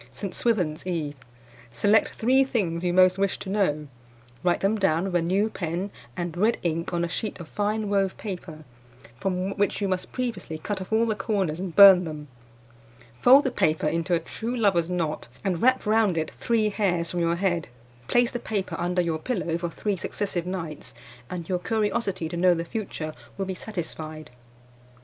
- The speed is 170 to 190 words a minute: Yes, average, 185 wpm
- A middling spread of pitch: Yes, average, 3.7 semitones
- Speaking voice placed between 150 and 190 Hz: Yes, medium, 185 Hz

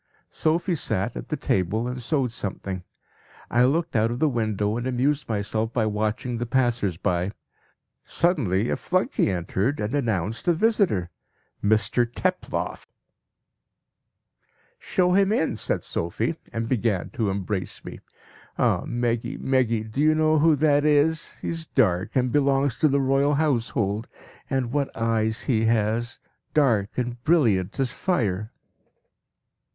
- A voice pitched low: Yes, low, 120 Hz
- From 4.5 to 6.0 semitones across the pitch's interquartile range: Yes, average, 5.1 semitones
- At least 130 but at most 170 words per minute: Yes, average, 140 wpm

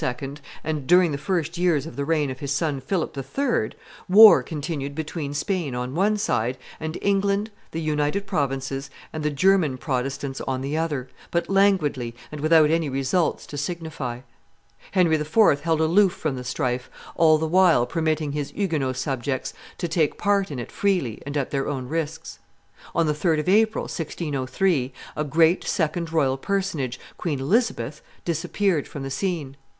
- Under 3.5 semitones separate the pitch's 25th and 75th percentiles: No, average, 4.2 semitones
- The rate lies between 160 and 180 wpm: Yes, average, 165 wpm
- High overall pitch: No, medium, 155 Hz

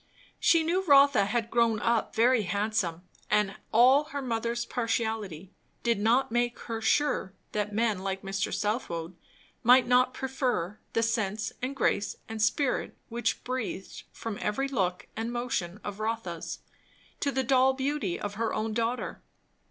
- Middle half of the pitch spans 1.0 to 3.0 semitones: No, average, 3.4 semitones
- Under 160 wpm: Yes, average, 150 wpm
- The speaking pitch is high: Yes, high, 225 Hz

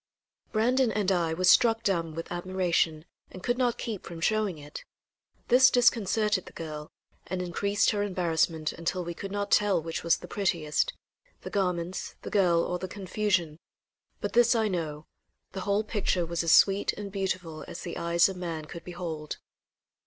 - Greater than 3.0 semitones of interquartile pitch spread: Yes, average, 3.5 semitones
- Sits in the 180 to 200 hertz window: Yes, medium, 185 Hz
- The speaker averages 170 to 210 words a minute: Yes, average, 175 wpm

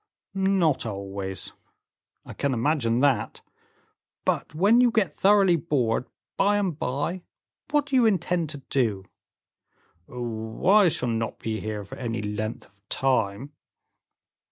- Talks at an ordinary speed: No, slow, 130 wpm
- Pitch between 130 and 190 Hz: Yes, low, 135 Hz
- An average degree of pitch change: No, wide, 9.0 semitones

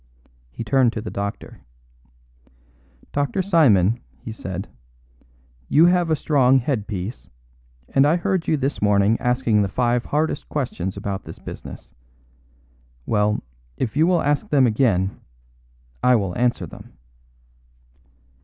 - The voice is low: Yes, low, 125 Hz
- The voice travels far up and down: Yes, wide, 6.1 semitones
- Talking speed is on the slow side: Yes, slow, 130 wpm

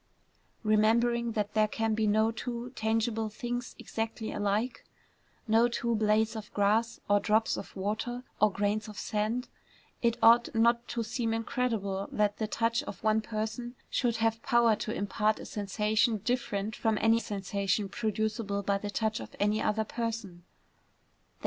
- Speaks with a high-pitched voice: Yes, high, 220 Hz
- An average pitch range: No, narrow, 1.6 semitones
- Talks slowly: No, average, 155 wpm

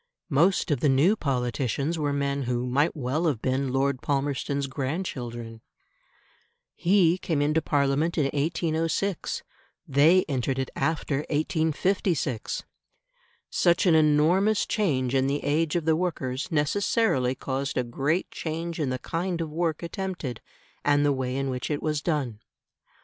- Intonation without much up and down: No, average, 3.7 semitones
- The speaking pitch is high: No, medium, 145 Hz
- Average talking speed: Yes, average, 145 wpm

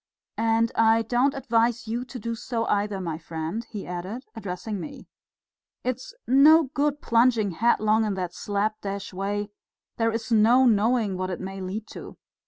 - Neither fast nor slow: Yes, average, 160 wpm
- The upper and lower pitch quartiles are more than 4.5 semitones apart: No, average, 3.2 semitones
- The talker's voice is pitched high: Yes, high, 220 Hz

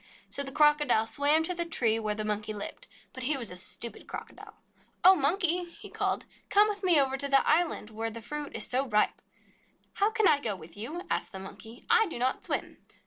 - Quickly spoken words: Yes, fast, 220 wpm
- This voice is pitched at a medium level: No, very high, 275 Hz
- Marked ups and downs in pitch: Yes, wide, 7.4 semitones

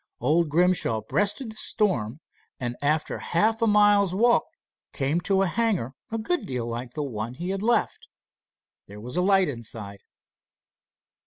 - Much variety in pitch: Yes, wide, 8.8 semitones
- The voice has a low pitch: No, medium, 170 Hz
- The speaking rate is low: No, average, 155 wpm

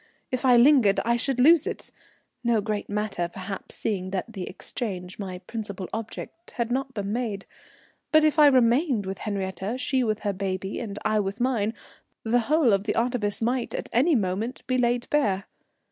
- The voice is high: Yes, high, 225 Hz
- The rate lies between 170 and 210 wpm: Yes, average, 180 wpm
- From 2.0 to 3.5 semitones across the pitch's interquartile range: No, average, 4.2 semitones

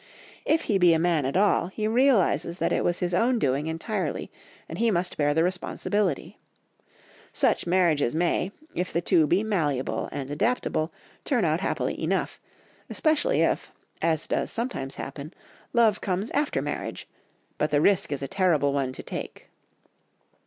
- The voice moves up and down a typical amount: No, wide, 5.7 semitones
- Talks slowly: No, average, 160 wpm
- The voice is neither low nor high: Yes, medium, 175 Hz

